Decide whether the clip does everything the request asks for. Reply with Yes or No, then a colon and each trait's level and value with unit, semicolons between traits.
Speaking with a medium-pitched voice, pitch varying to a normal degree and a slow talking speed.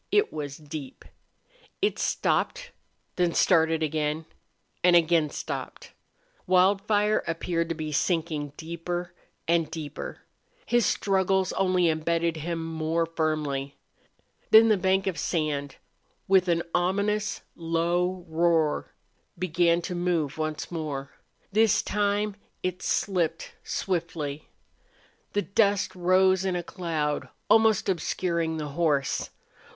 Yes: medium, 170 Hz; average, 3.0 semitones; slow, 115 wpm